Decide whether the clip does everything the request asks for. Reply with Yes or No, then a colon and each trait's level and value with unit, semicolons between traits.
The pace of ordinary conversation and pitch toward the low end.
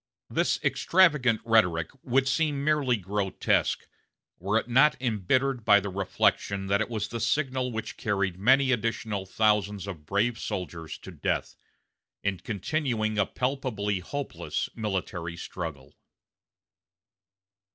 No: slow, 120 wpm; low, 110 Hz